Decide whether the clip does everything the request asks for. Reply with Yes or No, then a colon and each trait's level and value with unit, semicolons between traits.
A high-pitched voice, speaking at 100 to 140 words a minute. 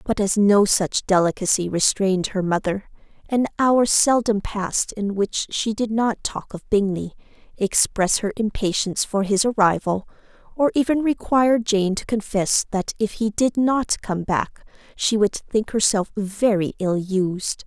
No: high, 210 Hz; average, 155 wpm